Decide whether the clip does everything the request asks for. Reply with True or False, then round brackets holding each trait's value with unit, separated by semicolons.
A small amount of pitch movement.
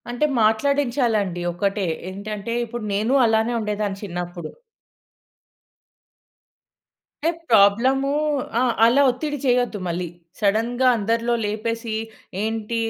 False (3.1 semitones)